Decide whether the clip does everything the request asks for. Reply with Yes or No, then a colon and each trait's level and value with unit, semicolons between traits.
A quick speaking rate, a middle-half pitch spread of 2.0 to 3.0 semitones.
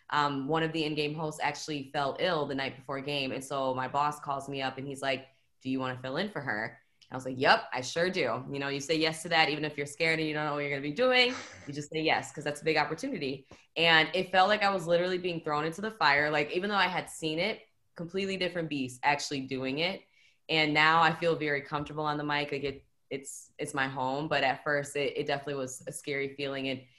Yes: fast, 265 wpm; narrow, 2.6 semitones